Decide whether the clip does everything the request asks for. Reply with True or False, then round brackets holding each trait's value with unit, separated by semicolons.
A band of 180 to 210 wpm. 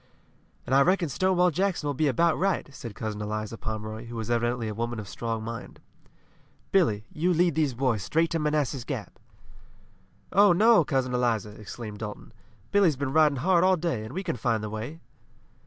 True (185 wpm)